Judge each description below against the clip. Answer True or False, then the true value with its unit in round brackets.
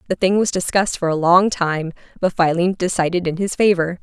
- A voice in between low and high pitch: True (180 Hz)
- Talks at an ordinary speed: False (210 wpm)